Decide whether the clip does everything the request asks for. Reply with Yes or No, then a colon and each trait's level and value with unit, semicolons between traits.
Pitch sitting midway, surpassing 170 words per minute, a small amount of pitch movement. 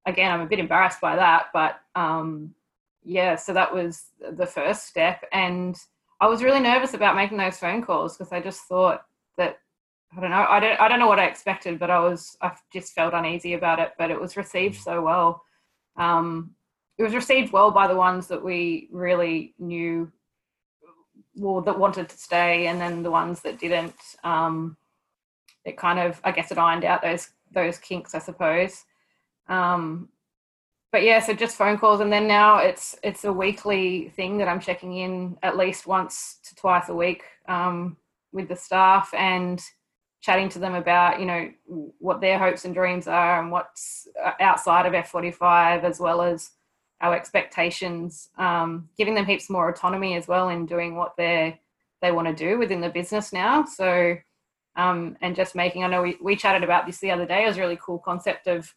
Yes: medium, 180 Hz; average, 195 wpm; narrow, 1.9 semitones